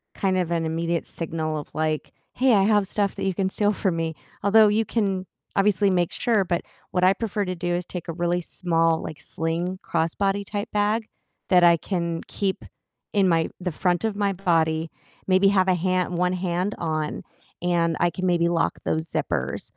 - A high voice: No, medium, 180 Hz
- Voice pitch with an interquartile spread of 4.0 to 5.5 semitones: No, average, 2.9 semitones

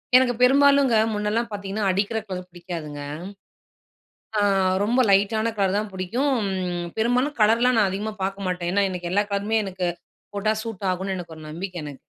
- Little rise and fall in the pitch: No, average, 3.5 semitones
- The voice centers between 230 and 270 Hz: No, high, 200 Hz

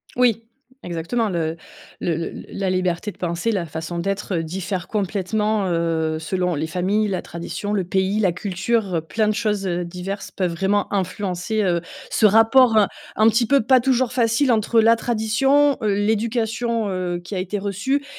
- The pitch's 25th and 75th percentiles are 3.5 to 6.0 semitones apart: Yes, average, 4.0 semitones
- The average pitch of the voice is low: No, high, 200 Hz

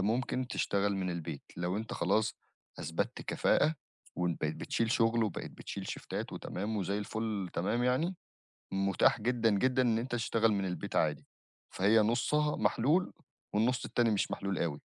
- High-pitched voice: No, low, 110 Hz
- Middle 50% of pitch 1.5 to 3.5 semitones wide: No, average, 3.9 semitones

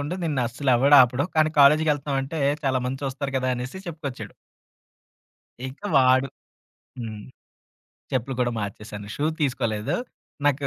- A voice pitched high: No, low, 135 Hz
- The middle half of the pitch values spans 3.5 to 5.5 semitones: No, narrow, 2.6 semitones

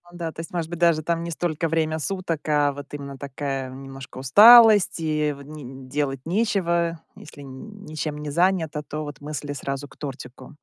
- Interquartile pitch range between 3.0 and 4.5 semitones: Yes, average, 3.3 semitones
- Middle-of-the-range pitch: Yes, medium, 150 Hz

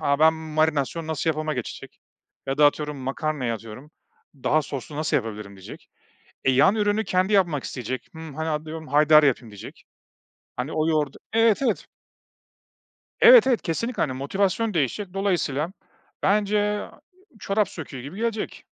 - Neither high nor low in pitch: Yes, medium, 155 Hz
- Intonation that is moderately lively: No, wide, 5.8 semitones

